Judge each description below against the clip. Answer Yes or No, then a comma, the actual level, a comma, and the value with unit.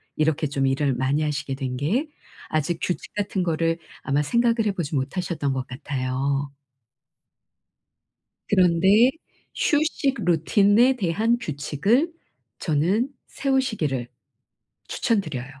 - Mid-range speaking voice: Yes, medium, 165 Hz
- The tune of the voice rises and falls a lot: Yes, wide, 7.3 semitones